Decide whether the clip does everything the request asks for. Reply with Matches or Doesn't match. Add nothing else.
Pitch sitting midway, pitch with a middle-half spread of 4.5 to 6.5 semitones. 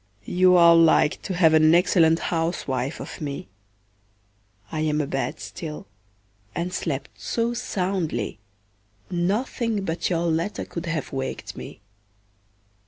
Doesn't match